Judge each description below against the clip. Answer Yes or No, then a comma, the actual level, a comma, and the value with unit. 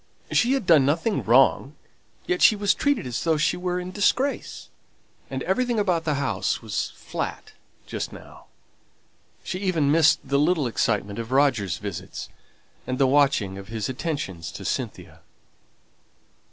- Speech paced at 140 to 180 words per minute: Yes, average, 150 wpm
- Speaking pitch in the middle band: Yes, medium, 145 Hz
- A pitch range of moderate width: No, wide, 7.5 semitones